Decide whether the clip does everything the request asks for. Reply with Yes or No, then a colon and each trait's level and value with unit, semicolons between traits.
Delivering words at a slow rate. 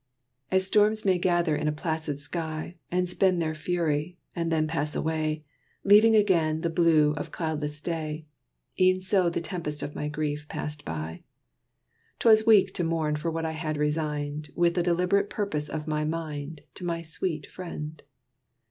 No: average, 170 wpm